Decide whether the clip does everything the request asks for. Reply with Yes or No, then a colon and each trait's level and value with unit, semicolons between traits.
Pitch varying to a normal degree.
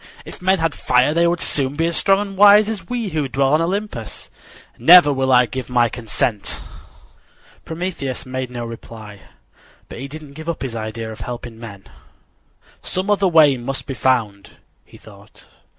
No: wide, 6.1 semitones